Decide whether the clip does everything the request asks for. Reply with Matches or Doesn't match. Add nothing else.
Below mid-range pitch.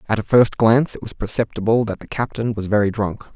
Matches